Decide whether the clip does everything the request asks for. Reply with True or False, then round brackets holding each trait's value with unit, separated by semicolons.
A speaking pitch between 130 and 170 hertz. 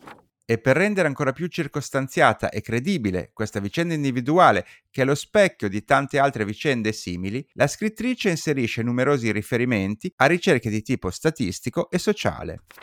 True (135 Hz)